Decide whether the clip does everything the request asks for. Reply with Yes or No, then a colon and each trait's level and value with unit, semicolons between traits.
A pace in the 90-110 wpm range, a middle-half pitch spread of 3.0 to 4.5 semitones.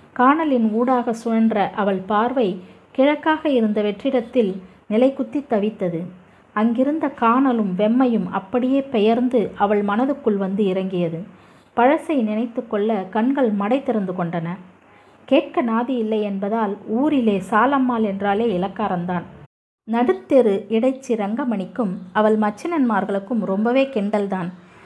Yes: average, 100 wpm; average, 4.1 semitones